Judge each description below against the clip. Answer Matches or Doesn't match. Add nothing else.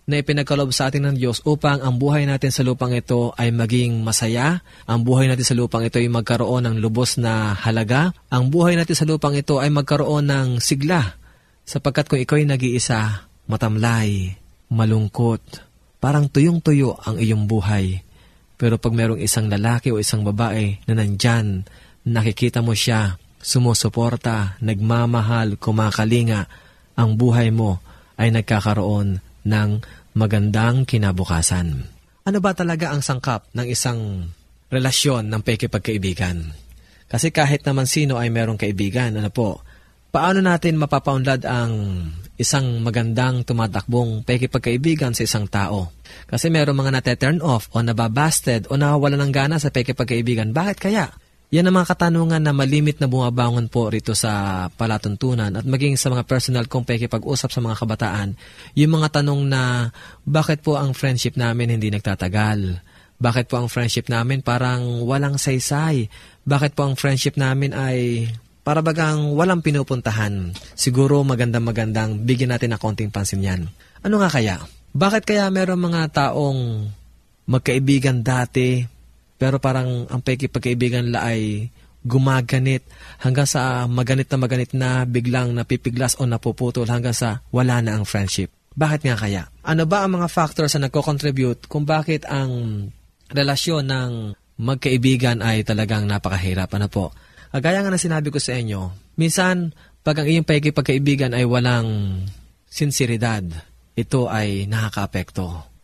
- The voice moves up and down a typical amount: Matches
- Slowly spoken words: Doesn't match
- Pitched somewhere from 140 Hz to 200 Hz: Doesn't match